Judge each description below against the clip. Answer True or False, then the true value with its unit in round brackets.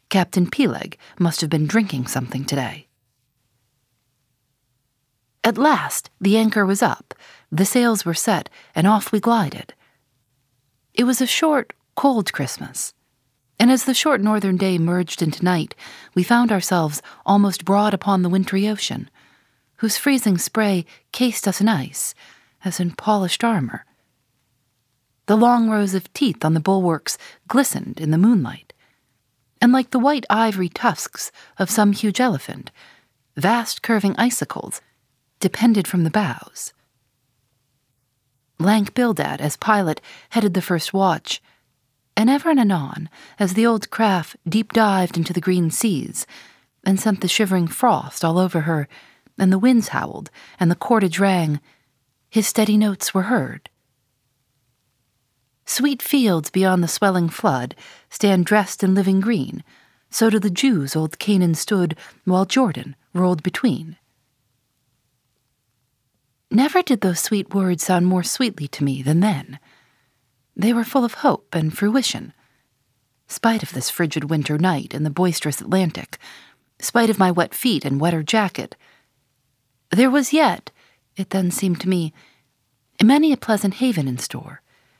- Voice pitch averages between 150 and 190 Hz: True (185 Hz)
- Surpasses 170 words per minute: False (145 wpm)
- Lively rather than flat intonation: True (8.0 semitones)